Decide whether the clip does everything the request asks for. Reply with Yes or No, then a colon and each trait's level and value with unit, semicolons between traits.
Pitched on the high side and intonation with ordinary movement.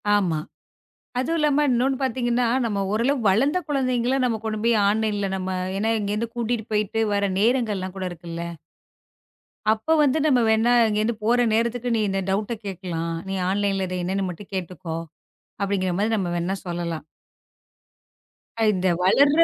Yes: high, 215 Hz; average, 4.2 semitones